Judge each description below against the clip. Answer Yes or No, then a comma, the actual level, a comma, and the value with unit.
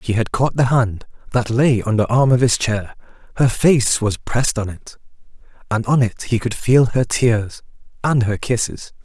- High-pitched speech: No, low, 115 Hz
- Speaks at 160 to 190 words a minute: No, average, 200 wpm